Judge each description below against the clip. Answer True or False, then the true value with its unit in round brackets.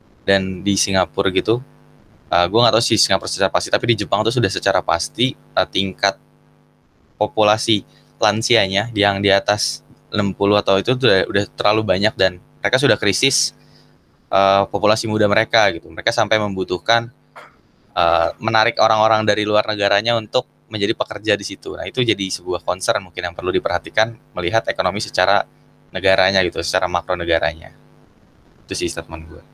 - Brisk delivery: True (155 wpm)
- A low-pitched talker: True (100 Hz)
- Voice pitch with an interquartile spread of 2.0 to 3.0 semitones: True (2.6 semitones)